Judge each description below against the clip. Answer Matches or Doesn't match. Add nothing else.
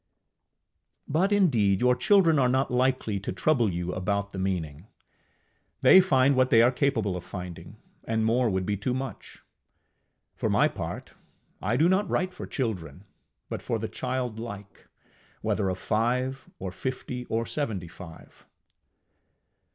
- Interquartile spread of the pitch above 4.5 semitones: Matches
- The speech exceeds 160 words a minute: Doesn't match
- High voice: Doesn't match